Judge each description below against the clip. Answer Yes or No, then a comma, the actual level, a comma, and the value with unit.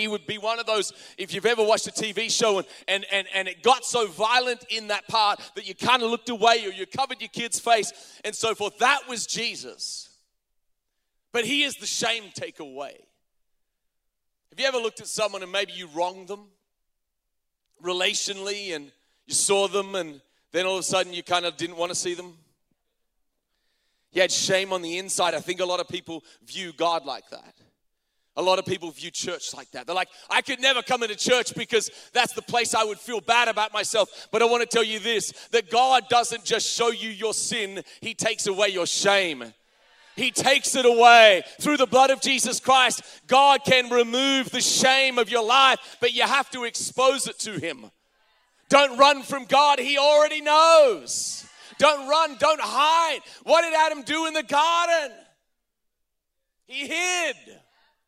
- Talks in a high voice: Yes, high, 225 Hz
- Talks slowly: No, average, 190 wpm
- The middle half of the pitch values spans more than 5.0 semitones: Yes, wide, 5.5 semitones